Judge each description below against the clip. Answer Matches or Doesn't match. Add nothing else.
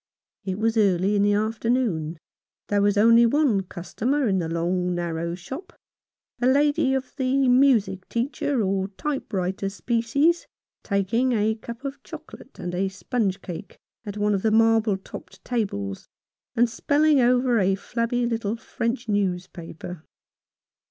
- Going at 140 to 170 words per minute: Matches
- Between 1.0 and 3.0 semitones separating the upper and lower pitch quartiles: Doesn't match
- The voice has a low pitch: Doesn't match